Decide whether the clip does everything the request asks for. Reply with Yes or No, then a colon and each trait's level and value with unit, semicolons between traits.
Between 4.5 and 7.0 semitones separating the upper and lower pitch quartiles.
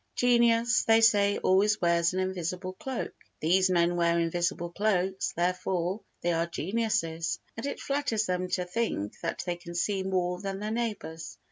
No: average, 3.7 semitones